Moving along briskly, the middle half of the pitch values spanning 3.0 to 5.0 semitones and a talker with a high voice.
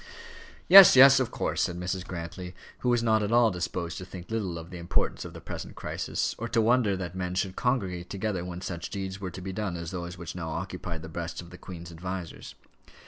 No: fast, 225 wpm; average, 3.3 semitones; very low, 90 Hz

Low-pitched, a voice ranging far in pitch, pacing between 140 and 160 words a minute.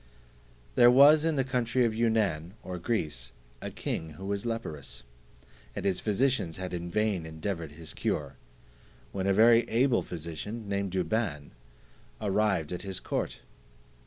Yes: low, 100 Hz; wide, 5.7 semitones; average, 145 wpm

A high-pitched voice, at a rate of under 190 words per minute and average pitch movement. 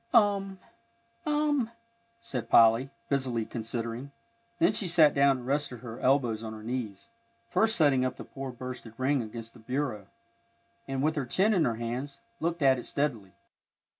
No: low, 130 Hz; average, 165 wpm; average, 4.0 semitones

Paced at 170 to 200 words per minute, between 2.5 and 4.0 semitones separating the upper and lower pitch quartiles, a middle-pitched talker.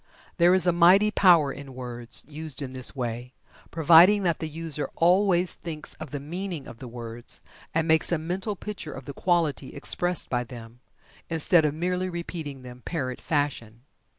No: average, 175 wpm; average, 5.1 semitones; medium, 155 Hz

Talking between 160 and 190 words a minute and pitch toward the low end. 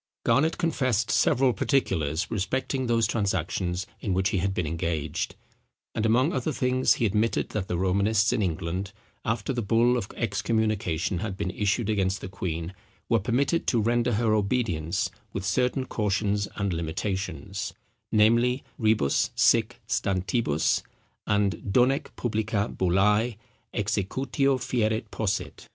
No: slow, 135 wpm; low, 105 Hz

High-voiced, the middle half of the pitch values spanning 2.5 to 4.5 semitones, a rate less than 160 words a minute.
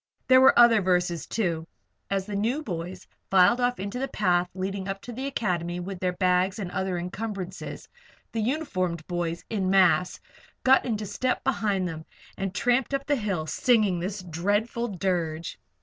No: high, 195 Hz; average, 4.1 semitones; average, 170 wpm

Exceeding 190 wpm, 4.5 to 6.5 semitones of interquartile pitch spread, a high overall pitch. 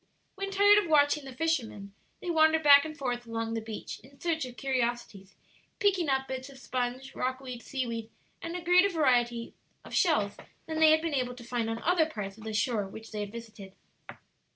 Yes: average, 200 wpm; wide, 5.5 semitones; very high, 260 Hz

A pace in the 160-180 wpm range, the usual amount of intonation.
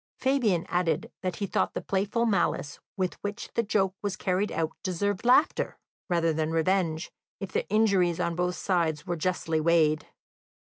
Yes: average, 165 wpm; average, 3.4 semitones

